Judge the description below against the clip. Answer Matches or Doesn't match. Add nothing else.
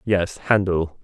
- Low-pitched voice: Matches